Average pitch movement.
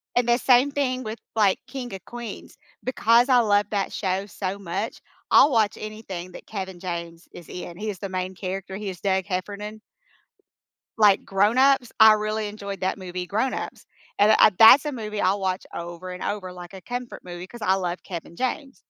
Yes: average, 3.3 semitones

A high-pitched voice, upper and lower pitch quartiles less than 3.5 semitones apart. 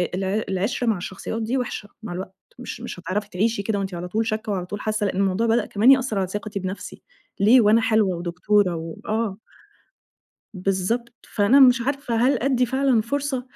No: high, 215 Hz; average, 3.8 semitones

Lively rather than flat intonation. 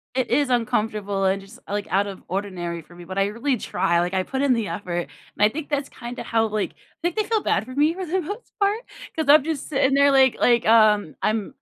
Yes: wide, 6.2 semitones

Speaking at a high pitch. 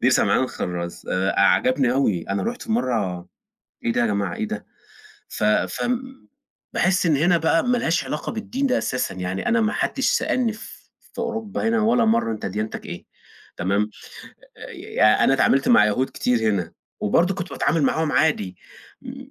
No: low, 135 Hz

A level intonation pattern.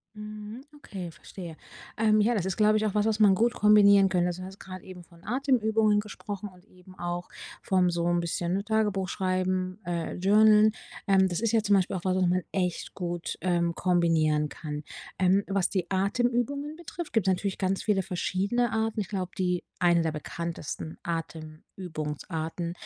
No: average, 3.3 semitones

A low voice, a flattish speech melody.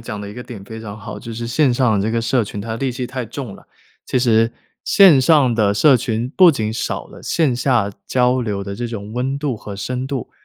No: low, 120 Hz; average, 3.0 semitones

